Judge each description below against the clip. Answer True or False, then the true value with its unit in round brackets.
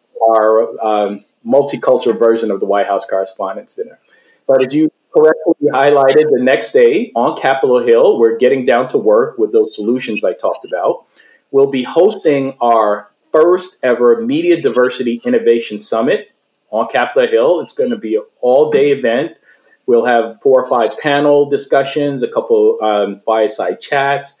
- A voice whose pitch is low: False (145 Hz)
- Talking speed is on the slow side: False (160 wpm)